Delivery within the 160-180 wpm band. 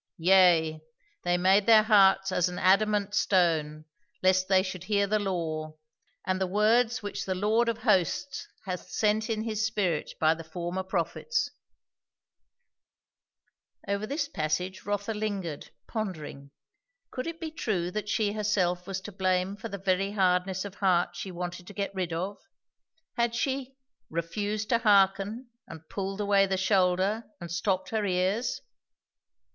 No: average, 150 wpm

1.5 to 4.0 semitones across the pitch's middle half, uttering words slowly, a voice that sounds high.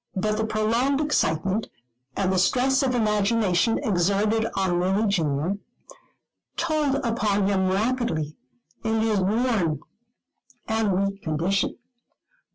Yes: average, 3.4 semitones; slow, 110 wpm; high, 210 Hz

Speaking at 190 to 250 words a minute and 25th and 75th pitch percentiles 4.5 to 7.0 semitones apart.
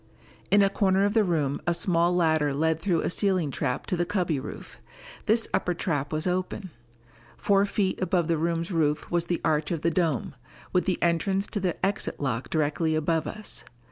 No: average, 195 wpm; average, 3.2 semitones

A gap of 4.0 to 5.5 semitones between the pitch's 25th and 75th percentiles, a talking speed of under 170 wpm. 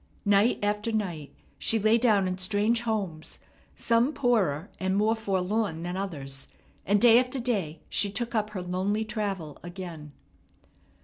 No: average, 3.6 semitones; average, 145 wpm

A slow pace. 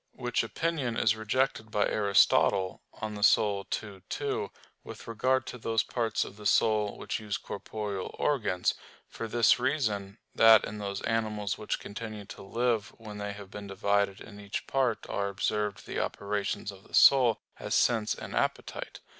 No: average, 165 wpm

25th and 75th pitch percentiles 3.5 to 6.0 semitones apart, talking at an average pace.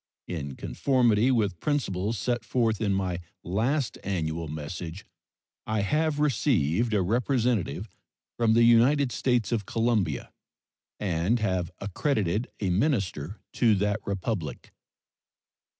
No: average, 4.9 semitones; slow, 115 wpm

